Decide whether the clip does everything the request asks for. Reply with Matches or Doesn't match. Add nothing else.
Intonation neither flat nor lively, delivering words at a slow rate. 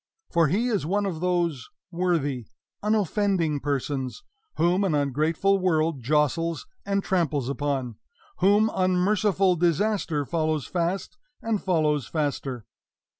Matches